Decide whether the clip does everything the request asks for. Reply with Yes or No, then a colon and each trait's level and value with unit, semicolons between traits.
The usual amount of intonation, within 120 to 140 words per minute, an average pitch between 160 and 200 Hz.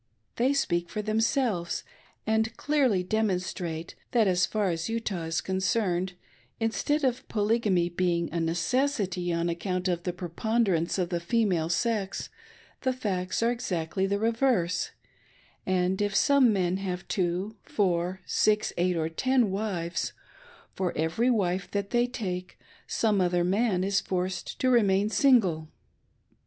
Yes: average, 4.2 semitones; slow, 135 wpm; high, 190 Hz